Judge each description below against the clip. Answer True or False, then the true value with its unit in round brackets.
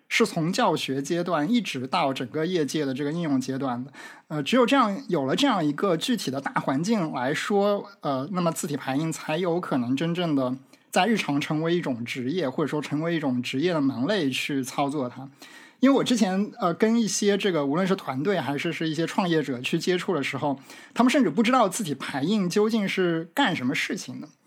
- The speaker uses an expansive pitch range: True (7.1 semitones)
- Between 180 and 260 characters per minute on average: False (315 characters per minute)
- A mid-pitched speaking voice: True (170 Hz)